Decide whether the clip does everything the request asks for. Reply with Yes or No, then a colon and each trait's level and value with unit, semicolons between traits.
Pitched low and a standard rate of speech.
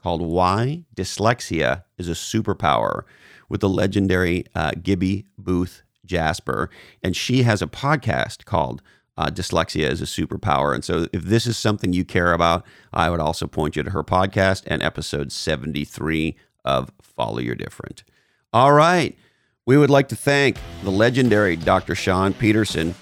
Yes: very low, 90 Hz; average, 155 wpm